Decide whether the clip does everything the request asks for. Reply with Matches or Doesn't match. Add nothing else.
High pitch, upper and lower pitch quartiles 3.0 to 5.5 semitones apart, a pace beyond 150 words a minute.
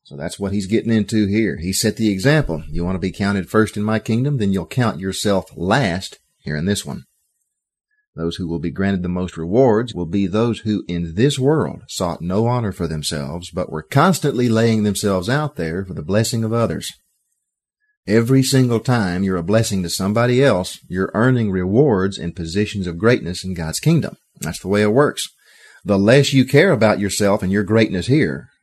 Doesn't match